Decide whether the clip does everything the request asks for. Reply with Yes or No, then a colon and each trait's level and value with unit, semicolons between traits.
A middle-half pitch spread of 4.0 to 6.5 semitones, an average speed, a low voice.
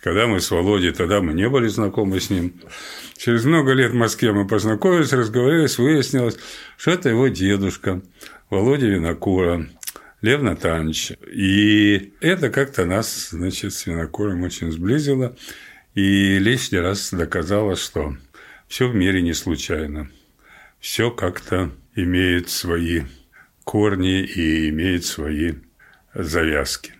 Yes: average, 4.9 semitones; average, 125 wpm; very low, 95 Hz